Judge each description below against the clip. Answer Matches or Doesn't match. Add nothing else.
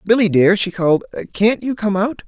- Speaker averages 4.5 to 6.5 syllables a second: Matches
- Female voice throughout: Doesn't match